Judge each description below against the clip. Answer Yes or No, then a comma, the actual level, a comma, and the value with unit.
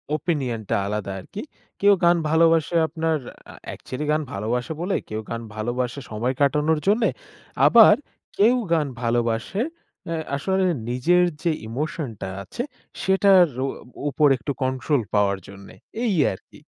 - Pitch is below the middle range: No, medium, 145 Hz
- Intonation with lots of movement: Yes, wide, 6.8 semitones